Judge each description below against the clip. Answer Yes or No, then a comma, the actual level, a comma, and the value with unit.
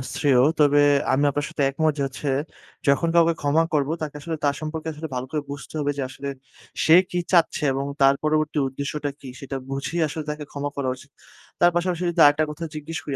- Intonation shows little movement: Yes, narrow, 2.1 semitones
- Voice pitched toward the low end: No, medium, 150 Hz